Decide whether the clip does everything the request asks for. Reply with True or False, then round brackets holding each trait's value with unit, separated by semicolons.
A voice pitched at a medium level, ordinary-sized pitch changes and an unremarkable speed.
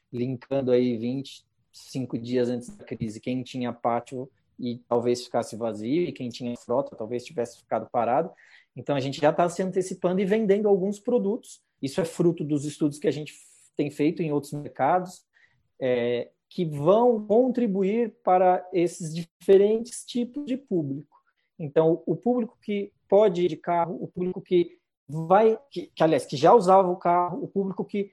False (170 Hz; 7.4 semitones; 170 wpm)